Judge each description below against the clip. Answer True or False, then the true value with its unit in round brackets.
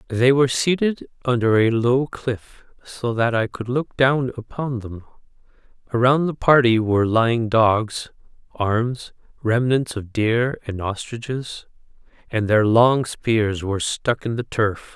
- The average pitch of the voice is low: True (120 Hz)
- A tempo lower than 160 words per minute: True (145 wpm)